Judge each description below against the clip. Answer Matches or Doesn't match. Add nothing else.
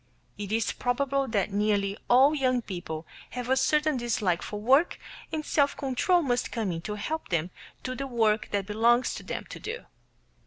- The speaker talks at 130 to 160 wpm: Doesn't match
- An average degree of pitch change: Matches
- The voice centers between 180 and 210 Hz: Doesn't match